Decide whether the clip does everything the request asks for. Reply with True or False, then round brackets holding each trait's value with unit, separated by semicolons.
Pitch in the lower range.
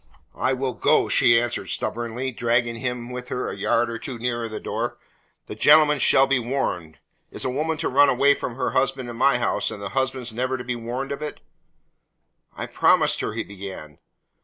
True (125 Hz)